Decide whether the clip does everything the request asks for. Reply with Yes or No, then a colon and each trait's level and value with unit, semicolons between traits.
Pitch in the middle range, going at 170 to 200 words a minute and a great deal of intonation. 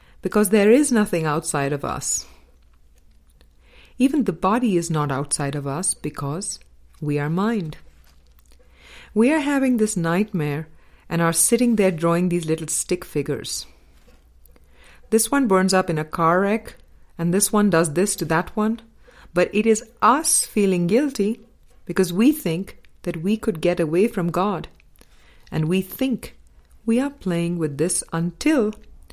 No: medium, 175 Hz; average, 150 wpm; wide, 6.5 semitones